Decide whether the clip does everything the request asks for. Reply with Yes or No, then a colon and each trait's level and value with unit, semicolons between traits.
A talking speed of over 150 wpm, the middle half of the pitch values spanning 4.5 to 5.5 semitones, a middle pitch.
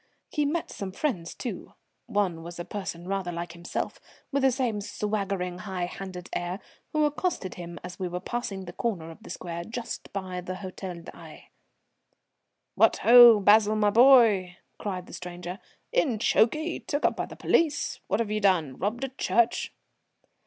No: average, 165 wpm; average, 4.8 semitones; high, 195 Hz